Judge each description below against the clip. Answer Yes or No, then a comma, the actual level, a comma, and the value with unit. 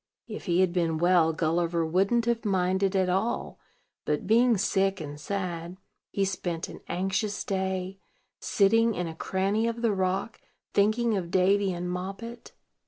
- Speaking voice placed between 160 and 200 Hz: Yes, high, 190 Hz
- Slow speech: No, average, 155 wpm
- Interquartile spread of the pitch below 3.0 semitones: Yes, narrow, 2.6 semitones